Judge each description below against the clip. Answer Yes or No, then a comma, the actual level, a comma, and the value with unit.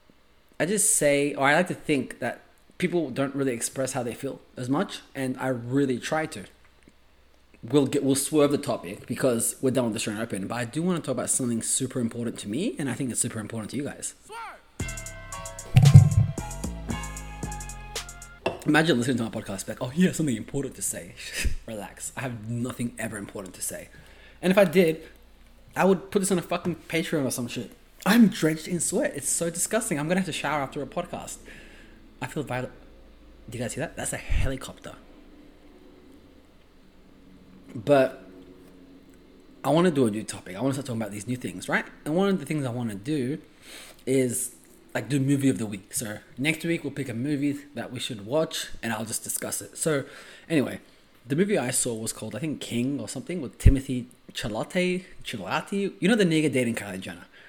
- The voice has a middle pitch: No, low, 130 Hz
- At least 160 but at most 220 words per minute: Yes, average, 200 wpm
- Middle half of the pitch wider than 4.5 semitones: Yes, average, 5.3 semitones